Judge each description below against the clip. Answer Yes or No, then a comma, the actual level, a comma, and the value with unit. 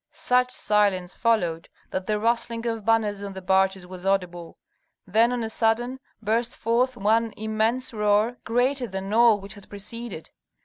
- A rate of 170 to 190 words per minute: No, average, 160 wpm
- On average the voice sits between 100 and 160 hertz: No, high, 220 Hz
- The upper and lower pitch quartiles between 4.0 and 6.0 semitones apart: No, average, 3.2 semitones